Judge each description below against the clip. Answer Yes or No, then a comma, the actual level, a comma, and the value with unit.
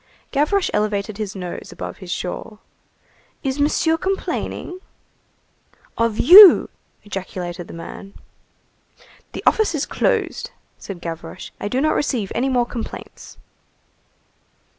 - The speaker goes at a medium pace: No, slow, 115 wpm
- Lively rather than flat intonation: Yes, wide, 7.6 semitones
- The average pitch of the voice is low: No, high, 220 Hz